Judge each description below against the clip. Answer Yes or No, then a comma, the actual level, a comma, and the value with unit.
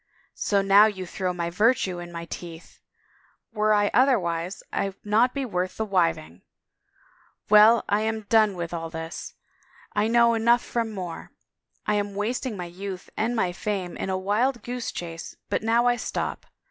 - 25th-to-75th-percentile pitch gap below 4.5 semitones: Yes, average, 4.0 semitones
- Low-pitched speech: No, high, 205 Hz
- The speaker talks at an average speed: Yes, average, 170 wpm